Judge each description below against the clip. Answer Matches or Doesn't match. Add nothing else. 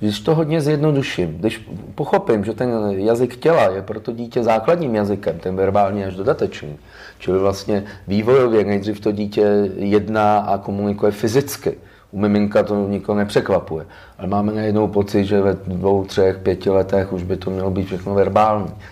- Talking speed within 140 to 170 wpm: Matches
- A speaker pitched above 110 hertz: Doesn't match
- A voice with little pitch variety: Matches